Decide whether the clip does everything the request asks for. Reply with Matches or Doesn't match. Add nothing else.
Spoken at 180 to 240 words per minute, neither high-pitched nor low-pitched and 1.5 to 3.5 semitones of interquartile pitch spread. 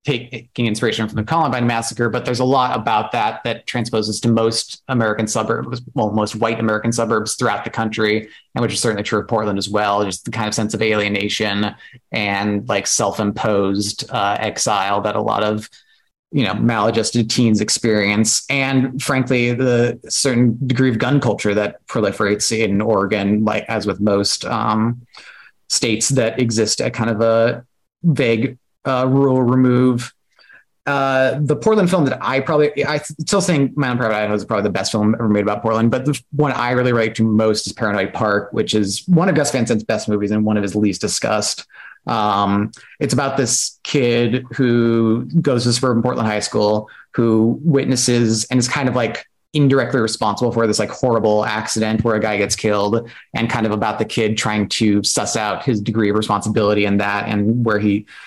Doesn't match